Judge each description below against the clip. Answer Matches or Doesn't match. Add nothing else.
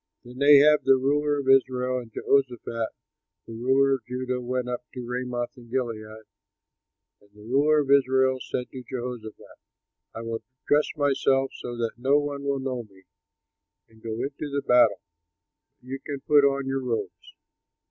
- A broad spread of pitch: Doesn't match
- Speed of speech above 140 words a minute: Matches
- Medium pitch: Doesn't match